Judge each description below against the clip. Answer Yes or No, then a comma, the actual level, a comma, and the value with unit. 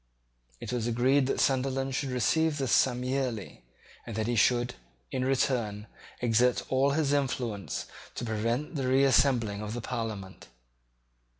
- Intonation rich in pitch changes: No, average, 2.9 semitones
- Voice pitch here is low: Yes, low, 125 Hz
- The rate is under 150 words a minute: Yes, average, 140 wpm